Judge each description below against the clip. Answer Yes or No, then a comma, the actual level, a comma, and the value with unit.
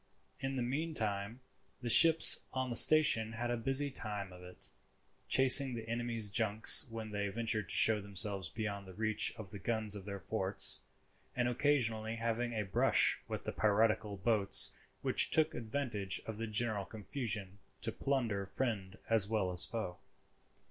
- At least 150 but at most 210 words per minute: Yes, average, 160 wpm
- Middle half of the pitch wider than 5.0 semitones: No, average, 3.0 semitones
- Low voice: Yes, low, 110 Hz